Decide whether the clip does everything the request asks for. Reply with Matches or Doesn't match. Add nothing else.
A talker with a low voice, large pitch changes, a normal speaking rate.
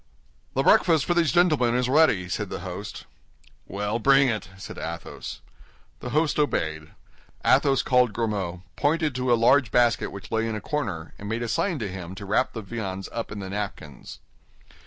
Matches